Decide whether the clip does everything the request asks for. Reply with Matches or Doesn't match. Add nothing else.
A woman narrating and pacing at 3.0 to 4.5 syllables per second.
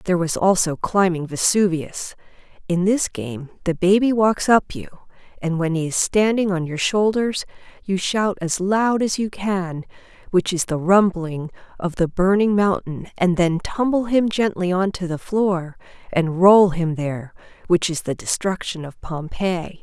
Matches